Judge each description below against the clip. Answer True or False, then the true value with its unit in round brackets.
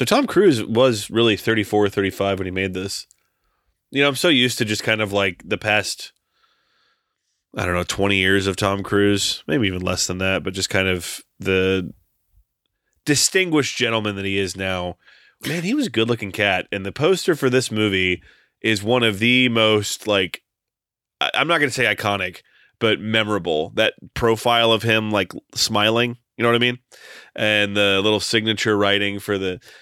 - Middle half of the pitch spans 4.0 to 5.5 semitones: False (3.2 semitones)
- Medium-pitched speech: False (105 Hz)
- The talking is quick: False (180 wpm)